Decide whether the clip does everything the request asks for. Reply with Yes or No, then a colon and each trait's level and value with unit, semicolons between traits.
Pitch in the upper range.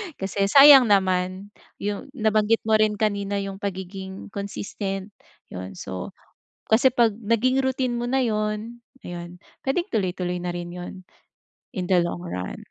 Yes: high, 200 Hz